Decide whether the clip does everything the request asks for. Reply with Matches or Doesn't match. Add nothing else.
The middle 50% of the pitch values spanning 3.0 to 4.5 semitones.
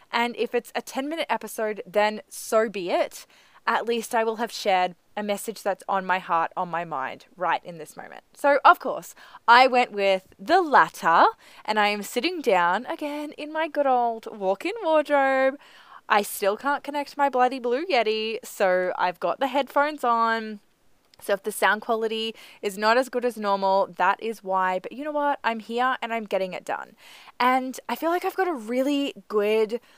Doesn't match